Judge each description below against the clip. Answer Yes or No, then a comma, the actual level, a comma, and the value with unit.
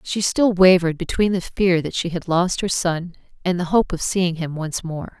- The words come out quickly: Yes, fast, 230 wpm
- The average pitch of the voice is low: No, medium, 175 Hz